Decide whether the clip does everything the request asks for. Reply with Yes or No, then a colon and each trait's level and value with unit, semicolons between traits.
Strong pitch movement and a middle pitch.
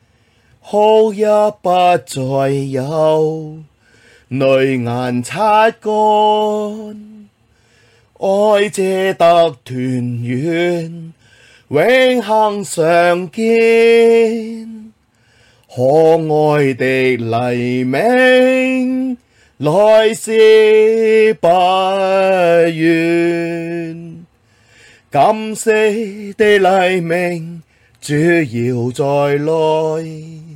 Yes: wide, 7.7 semitones; medium, 170 Hz